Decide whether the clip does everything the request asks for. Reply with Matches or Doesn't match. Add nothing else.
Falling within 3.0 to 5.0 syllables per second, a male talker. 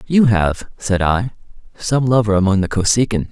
Matches